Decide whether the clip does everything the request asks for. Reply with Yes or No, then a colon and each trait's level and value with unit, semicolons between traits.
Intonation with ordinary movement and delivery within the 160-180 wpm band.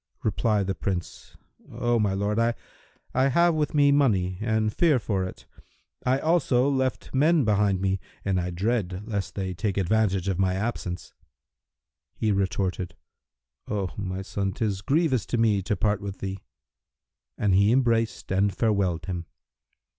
No: average, 3.9 semitones; average, 150 wpm